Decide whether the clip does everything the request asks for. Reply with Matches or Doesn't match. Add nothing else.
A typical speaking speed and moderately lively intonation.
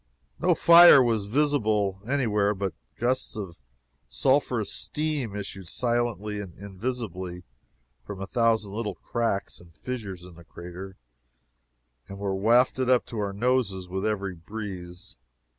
Doesn't match